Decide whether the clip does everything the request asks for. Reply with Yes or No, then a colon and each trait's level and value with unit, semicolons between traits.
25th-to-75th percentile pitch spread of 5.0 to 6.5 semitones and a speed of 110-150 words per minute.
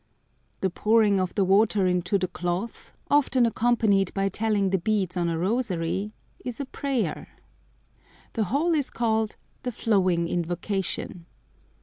No: average, 4.1 semitones; slow, 135 wpm